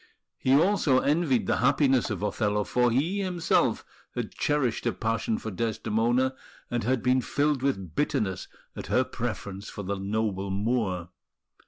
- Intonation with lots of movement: No, average, 4.8 semitones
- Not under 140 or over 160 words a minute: Yes, average, 150 wpm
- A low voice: Yes, low, 120 Hz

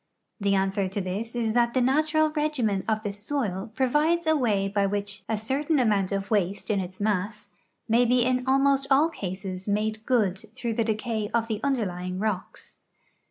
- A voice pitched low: No, high, 220 Hz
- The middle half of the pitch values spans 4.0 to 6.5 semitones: Yes, average, 4.4 semitones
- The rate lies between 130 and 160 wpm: No, average, 180 wpm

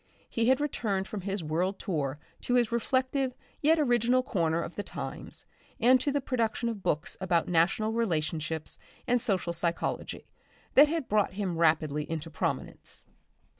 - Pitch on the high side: Yes, high, 205 Hz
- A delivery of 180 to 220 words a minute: No, average, 155 wpm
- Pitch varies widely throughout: Yes, wide, 6.7 semitones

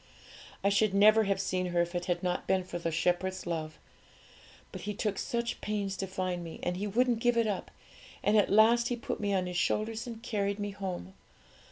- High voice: Yes, high, 195 Hz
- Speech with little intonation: No, average, 3.0 semitones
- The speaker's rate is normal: No, fast, 215 wpm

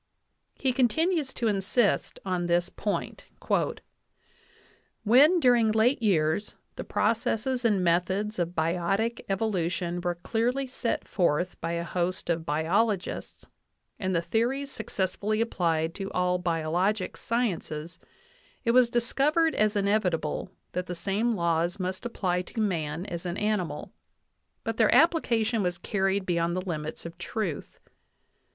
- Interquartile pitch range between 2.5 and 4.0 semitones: No, average, 4.8 semitones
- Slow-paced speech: Yes, slow, 130 wpm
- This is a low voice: No, high, 195 Hz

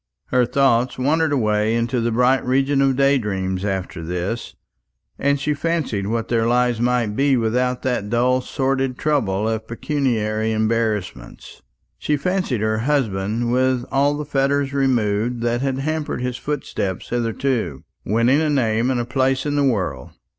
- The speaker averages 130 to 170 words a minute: Yes, average, 155 wpm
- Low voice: Yes, low, 125 Hz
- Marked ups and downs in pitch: No, average, 3.7 semitones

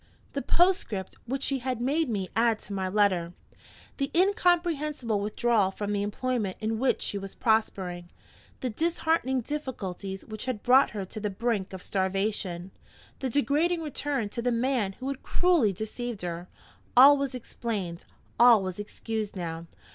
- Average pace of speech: Yes, average, 155 wpm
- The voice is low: No, high, 225 Hz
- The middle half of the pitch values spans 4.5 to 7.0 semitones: Yes, wide, 5.5 semitones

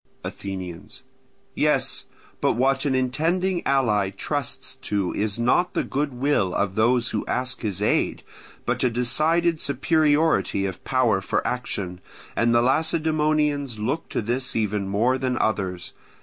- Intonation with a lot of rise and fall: Yes, wide, 5.9 semitones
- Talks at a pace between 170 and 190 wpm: No, slow, 135 wpm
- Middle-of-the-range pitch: No, low, 125 Hz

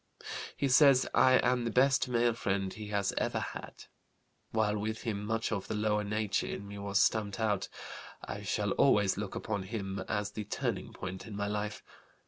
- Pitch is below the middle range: Yes, low, 105 Hz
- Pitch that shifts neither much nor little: No, narrow, 1.8 semitones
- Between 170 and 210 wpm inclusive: Yes, average, 185 wpm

